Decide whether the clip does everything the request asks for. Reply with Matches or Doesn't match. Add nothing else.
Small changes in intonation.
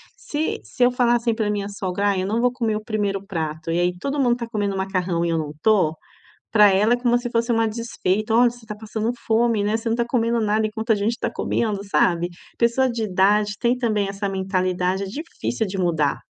Doesn't match